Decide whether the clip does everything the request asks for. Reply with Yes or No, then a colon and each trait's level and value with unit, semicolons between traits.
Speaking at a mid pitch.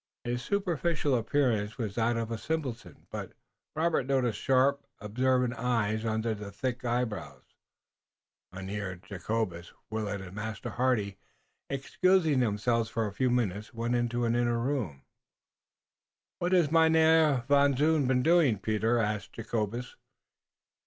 No: low, 120 Hz